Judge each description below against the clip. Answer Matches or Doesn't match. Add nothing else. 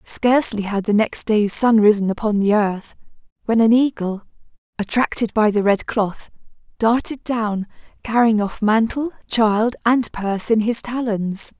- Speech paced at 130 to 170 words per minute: Matches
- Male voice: Doesn't match